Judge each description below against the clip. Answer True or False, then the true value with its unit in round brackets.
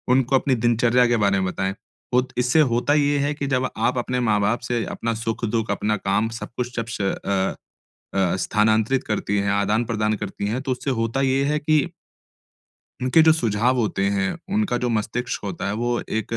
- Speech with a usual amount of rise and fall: True (3.4 semitones)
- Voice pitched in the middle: False (115 Hz)